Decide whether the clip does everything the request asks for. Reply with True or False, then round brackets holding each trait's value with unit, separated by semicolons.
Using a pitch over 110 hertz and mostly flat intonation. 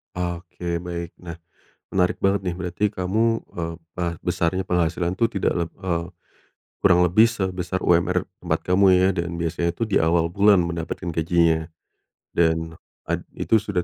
False (90 Hz; 1.7 semitones)